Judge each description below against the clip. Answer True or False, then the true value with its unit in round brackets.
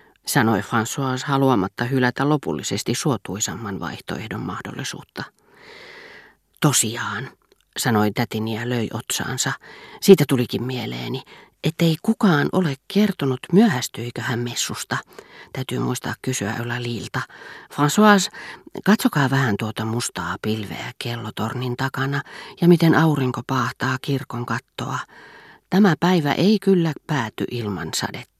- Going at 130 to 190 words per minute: False (105 wpm)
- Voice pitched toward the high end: False (130 Hz)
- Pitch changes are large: True (5.7 semitones)